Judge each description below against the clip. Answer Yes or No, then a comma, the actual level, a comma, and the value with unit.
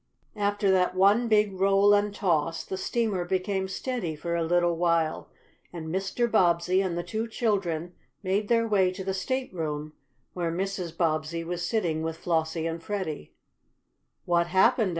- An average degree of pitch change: Yes, average, 3.2 semitones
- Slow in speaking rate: No, average, 155 wpm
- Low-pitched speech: No, medium, 185 Hz